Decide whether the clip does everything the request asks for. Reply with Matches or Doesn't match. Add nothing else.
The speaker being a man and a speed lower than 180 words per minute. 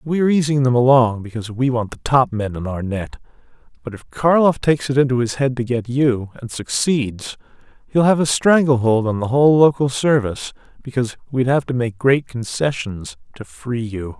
Doesn't match